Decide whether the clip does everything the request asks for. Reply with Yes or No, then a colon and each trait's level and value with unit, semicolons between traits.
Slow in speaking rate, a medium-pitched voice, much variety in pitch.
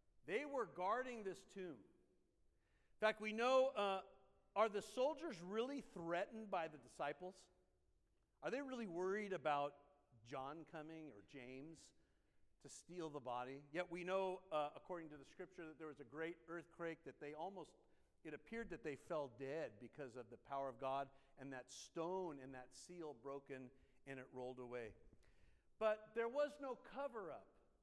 No: average, 165 wpm; medium, 160 Hz; wide, 6.0 semitones